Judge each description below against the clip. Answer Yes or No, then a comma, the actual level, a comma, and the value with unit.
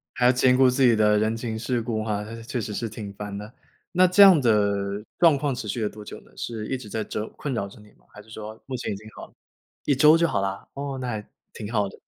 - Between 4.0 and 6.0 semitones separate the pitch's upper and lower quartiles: No, average, 3.4 semitones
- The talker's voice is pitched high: No, low, 110 Hz